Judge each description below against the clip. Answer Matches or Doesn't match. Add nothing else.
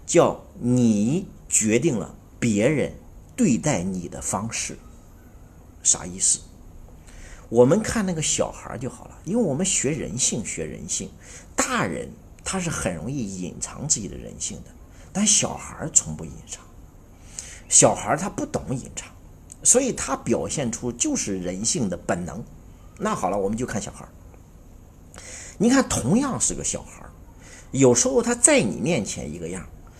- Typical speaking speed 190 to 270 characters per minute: Matches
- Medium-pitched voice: Doesn't match